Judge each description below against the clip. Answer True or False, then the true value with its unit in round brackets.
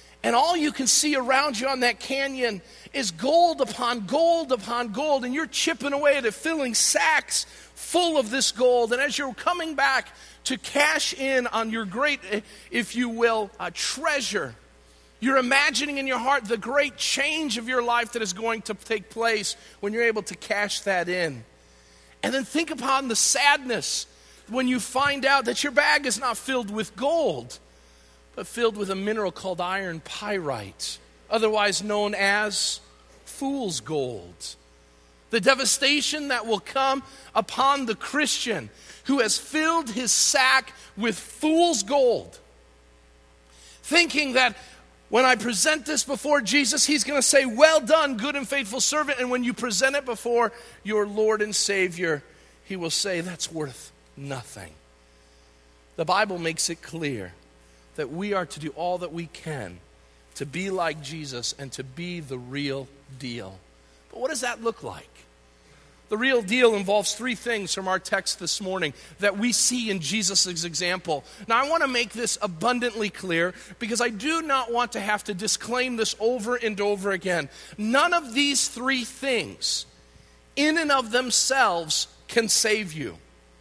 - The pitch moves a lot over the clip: True (7.9 semitones)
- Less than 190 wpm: True (165 wpm)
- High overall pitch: True (225 Hz)